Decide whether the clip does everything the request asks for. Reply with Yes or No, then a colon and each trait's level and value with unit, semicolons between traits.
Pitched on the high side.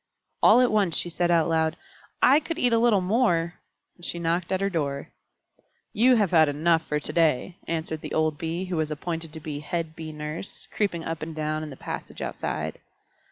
No: medium, 165 Hz